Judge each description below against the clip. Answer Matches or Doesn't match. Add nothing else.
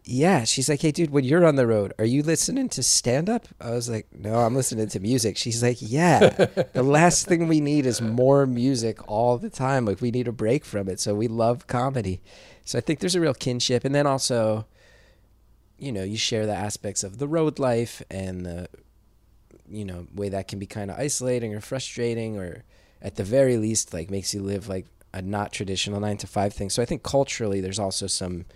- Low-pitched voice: Matches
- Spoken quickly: Matches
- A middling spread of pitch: Matches